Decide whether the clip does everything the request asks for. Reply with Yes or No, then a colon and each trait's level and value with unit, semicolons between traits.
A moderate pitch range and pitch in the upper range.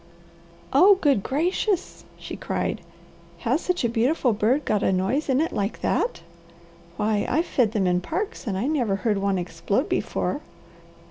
No: wide, 7.3 semitones; high, 240 Hz